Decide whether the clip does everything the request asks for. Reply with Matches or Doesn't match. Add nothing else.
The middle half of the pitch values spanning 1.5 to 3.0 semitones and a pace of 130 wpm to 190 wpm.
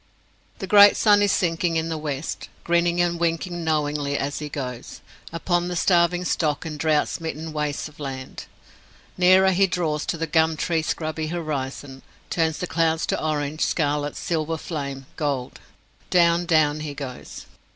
Matches